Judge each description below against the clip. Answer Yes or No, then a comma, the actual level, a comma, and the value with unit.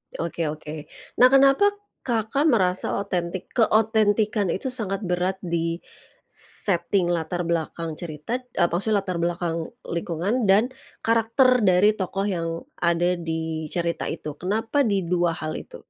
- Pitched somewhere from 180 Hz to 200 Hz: Yes, medium, 185 Hz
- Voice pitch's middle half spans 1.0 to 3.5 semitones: No, average, 4.5 semitones